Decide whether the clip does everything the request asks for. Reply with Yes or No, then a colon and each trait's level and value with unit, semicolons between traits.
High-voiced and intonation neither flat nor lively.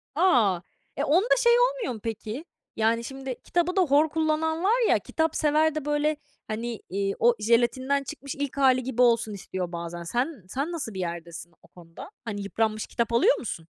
No: very high, 255 Hz; wide, 6.3 semitones